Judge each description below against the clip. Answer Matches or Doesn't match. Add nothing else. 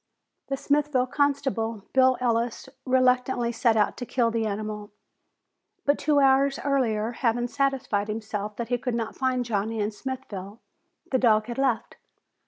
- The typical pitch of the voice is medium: Doesn't match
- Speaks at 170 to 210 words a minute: Doesn't match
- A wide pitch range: Doesn't match